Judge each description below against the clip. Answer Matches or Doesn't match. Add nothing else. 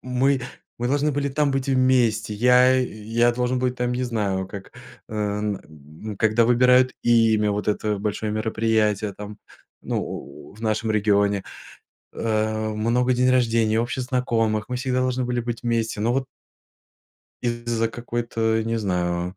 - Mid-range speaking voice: Doesn't match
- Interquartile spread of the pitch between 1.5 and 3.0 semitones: Matches